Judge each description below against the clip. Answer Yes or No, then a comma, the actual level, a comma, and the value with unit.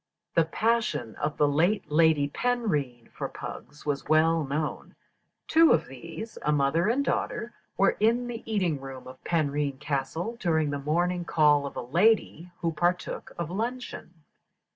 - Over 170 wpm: No, average, 155 wpm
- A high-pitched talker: No, medium, 160 Hz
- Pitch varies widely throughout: Yes, wide, 6.0 semitones